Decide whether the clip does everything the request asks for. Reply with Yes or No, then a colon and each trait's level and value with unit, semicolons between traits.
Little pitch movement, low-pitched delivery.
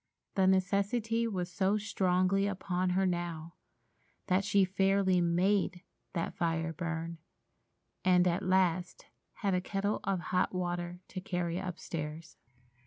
No: narrow, 2.0 semitones; medium, 185 Hz